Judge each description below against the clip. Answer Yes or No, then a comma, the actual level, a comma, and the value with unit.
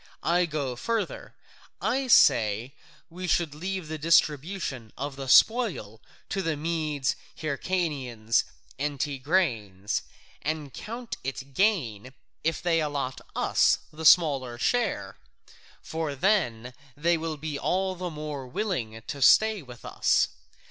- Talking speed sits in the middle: No, slow, 130 wpm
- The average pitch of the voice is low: No, medium, 150 Hz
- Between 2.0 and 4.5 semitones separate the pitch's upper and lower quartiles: No, wide, 5.4 semitones